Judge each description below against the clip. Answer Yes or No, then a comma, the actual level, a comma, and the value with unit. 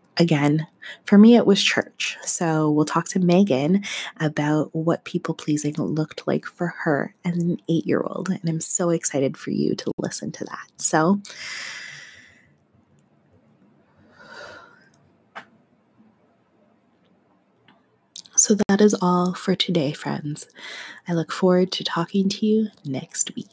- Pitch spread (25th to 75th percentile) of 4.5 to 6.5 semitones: No, average, 3.8 semitones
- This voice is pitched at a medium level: Yes, medium, 175 Hz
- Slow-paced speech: Yes, slow, 125 wpm